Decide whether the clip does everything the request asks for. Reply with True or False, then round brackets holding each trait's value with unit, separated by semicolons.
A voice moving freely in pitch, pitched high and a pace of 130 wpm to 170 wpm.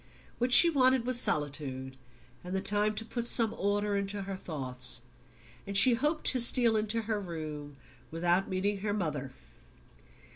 True (6.6 semitones; 200 Hz; 155 wpm)